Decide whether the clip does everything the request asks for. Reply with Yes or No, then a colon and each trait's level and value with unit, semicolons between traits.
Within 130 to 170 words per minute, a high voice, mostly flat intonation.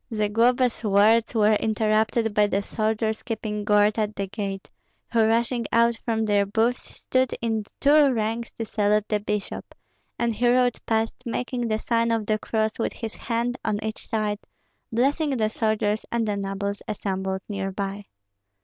Yes: average, 165 wpm; high, 220 Hz; narrow, 1.9 semitones